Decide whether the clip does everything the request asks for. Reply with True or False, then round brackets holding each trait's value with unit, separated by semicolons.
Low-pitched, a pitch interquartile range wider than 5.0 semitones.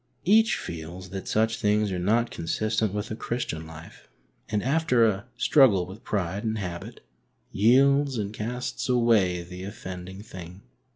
False (105 Hz; 4.3 semitones)